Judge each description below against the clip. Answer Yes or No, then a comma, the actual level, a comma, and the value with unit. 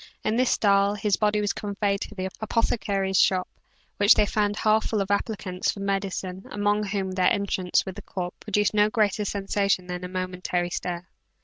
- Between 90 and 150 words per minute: No, average, 185 wpm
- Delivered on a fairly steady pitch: Yes, narrow, 1.9 semitones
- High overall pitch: Yes, high, 200 Hz